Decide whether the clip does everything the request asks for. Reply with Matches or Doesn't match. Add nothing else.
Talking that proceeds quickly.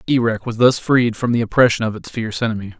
Matches